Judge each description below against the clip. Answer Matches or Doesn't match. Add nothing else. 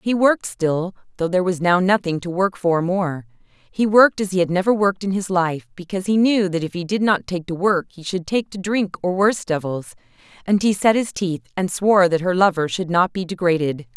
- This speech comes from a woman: Matches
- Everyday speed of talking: Doesn't match